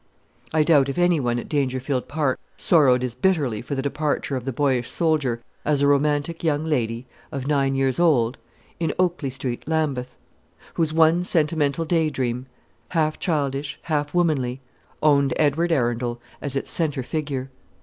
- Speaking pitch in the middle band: Yes, medium, 145 Hz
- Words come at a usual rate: Yes, average, 160 wpm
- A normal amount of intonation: Yes, average, 3.4 semitones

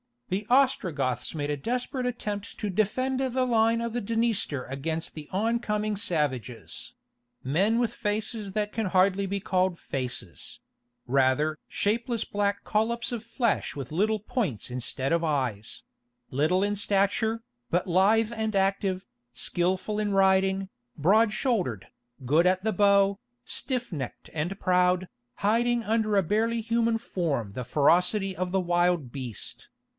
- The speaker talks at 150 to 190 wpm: No, slow, 135 wpm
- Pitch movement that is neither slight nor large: No, wide, 5.8 semitones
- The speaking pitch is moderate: No, high, 195 Hz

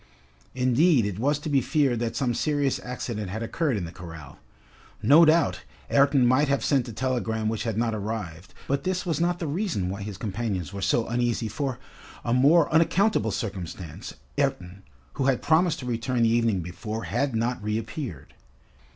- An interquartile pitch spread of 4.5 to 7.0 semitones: Yes, average, 5.0 semitones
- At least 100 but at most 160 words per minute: No, average, 175 wpm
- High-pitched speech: No, low, 120 Hz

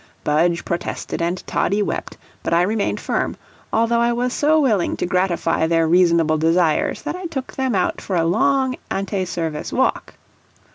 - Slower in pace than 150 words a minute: No, average, 170 wpm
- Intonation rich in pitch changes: Yes, wide, 5.9 semitones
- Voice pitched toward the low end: No, medium, 185 Hz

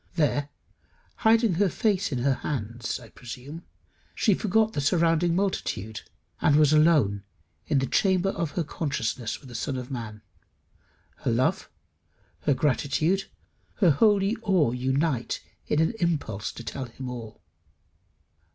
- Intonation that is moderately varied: No, wide, 6.0 semitones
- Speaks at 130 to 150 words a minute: Yes, average, 140 wpm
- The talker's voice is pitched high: No, medium, 145 Hz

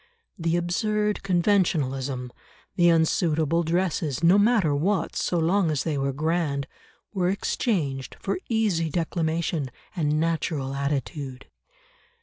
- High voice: No, medium, 165 Hz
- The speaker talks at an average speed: No, slow, 115 wpm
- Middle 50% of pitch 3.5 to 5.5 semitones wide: Yes, average, 3.9 semitones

